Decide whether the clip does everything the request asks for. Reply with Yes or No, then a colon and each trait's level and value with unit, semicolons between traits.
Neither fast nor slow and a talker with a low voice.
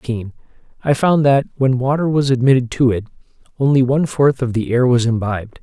Yes: average, 190 wpm; low, 130 Hz